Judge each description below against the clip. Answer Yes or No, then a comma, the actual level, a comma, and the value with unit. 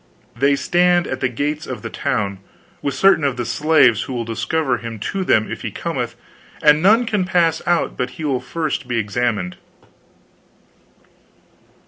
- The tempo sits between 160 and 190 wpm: Yes, average, 165 wpm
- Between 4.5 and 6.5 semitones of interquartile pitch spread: Yes, average, 5.3 semitones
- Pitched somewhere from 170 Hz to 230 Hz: No, medium, 140 Hz